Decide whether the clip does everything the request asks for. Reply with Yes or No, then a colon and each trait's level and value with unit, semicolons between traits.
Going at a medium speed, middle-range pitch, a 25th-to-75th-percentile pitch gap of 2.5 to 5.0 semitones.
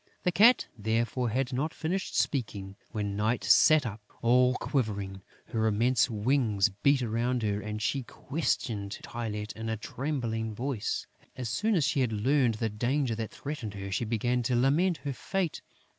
No: average, 165 wpm; low, 120 Hz; average, 4.1 semitones